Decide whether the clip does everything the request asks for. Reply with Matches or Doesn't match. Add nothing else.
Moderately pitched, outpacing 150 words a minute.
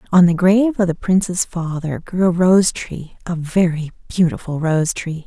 Matches